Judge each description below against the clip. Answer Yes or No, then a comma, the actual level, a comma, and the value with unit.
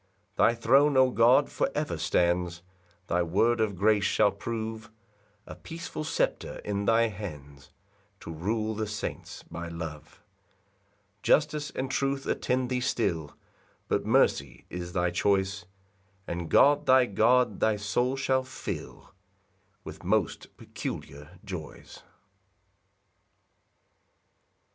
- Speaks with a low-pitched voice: Yes, low, 105 Hz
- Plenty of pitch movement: Yes, wide, 6.1 semitones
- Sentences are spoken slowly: Yes, slow, 120 wpm